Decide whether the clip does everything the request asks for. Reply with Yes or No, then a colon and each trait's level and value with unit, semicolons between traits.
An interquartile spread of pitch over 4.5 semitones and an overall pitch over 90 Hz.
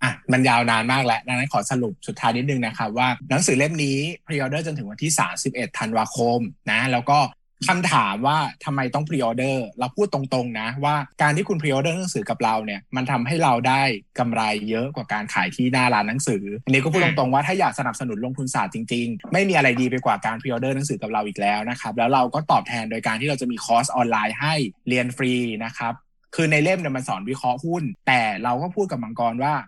No: average, 3.6 semitones; low, 130 Hz